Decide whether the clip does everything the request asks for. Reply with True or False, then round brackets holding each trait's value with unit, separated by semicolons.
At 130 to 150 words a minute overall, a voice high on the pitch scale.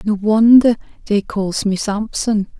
True (140 wpm; 210 Hz)